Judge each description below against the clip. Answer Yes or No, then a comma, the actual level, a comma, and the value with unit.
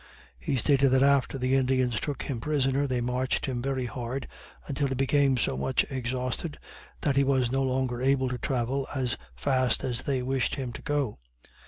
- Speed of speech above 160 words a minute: Yes, average, 185 wpm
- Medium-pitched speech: No, low, 130 Hz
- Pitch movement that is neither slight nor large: No, narrow, 1.6 semitones